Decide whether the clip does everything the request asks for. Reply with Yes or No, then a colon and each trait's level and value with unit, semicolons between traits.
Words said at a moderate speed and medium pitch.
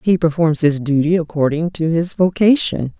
Yes: average, 160 wpm; medium, 165 Hz